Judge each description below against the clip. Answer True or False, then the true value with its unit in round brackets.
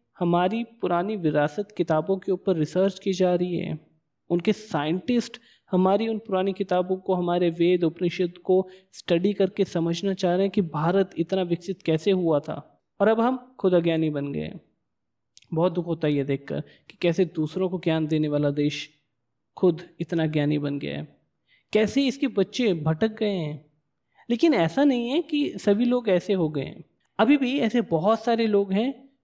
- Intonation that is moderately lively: True (4.3 semitones)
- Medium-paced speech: True (175 wpm)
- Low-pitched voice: False (185 Hz)